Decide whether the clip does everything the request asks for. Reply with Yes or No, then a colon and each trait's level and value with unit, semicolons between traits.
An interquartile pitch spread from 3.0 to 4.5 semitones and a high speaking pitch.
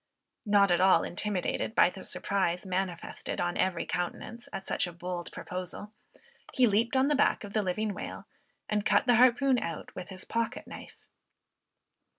Yes: average, 4.1 semitones; high, 200 Hz